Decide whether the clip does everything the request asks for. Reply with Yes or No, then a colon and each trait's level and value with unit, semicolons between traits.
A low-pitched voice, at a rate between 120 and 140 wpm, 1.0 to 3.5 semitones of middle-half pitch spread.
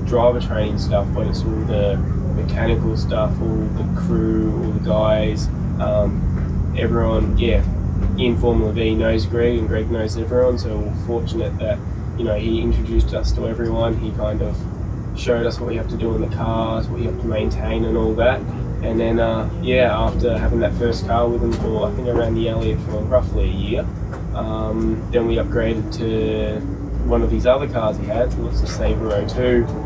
No: low, 110 Hz; average, 195 wpm; average, 2.8 semitones